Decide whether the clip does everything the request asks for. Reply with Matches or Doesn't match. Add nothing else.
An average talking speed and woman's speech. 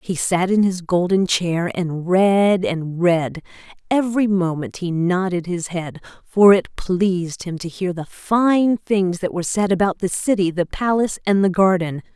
Matches